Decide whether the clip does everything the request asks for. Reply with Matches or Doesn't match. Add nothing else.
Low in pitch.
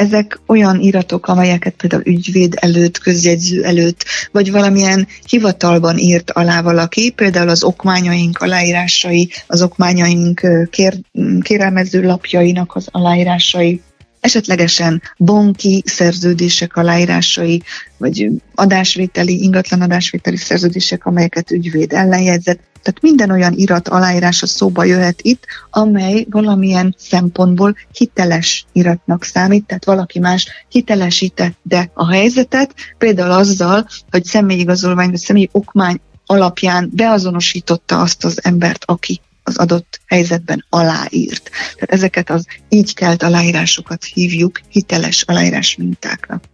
Doesn't match